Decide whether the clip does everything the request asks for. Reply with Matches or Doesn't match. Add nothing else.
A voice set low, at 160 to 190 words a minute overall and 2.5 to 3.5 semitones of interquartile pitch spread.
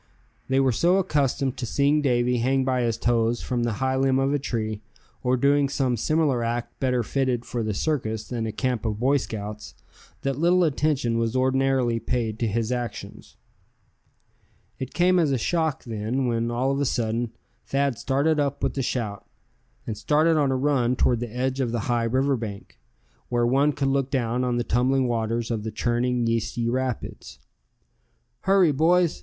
Matches